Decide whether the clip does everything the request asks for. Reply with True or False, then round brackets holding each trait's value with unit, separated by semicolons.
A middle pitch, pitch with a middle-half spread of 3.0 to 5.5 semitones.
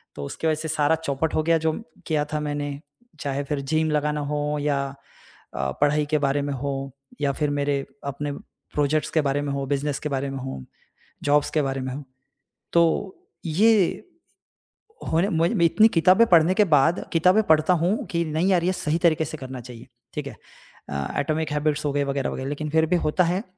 False (150 Hz; 2.4 semitones)